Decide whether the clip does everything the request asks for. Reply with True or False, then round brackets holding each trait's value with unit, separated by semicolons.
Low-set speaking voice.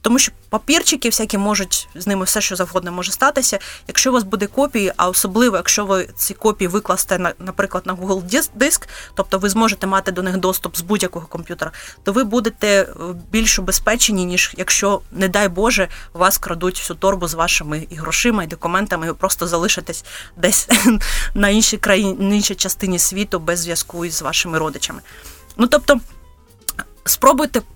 False (195 Hz)